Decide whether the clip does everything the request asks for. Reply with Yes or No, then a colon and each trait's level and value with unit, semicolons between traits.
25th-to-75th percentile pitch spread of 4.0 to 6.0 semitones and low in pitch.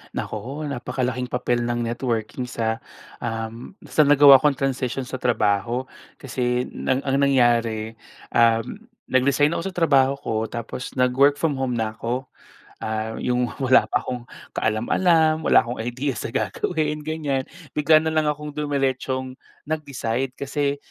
No: average, 3.3 semitones; low, 130 Hz